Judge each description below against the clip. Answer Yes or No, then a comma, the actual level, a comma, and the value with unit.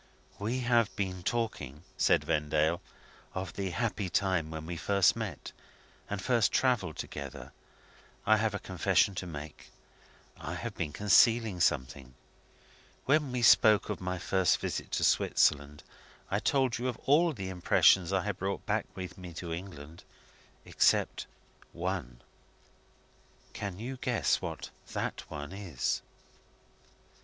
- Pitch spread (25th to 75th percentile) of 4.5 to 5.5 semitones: Yes, average, 4.8 semitones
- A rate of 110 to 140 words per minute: Yes, slow, 135 wpm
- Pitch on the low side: Yes, very low, 95 Hz